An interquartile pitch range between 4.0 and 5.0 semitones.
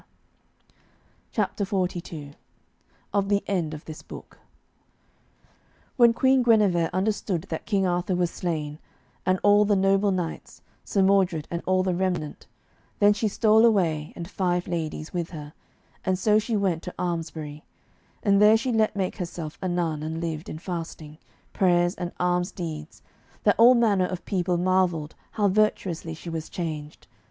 No: average, 3.5 semitones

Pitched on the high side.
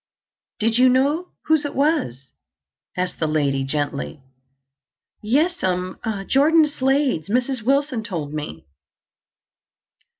Yes: high, 230 Hz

